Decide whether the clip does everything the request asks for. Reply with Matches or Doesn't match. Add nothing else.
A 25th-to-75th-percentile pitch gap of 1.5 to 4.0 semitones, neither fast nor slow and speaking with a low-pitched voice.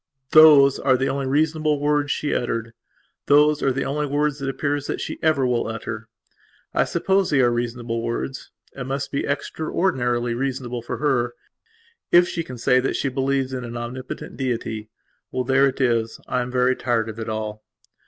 Matches